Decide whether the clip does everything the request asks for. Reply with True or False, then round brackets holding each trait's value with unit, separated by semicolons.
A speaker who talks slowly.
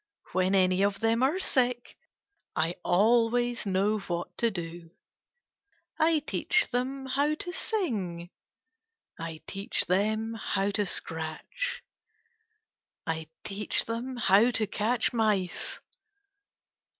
True (110 wpm)